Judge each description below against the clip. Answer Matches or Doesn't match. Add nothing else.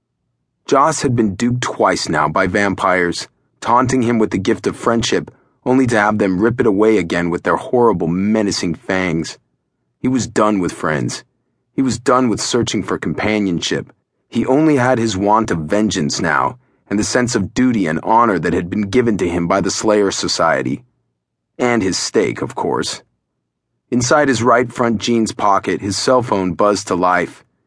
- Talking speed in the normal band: Matches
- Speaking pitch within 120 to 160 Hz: Doesn't match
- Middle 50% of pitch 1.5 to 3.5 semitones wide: Doesn't match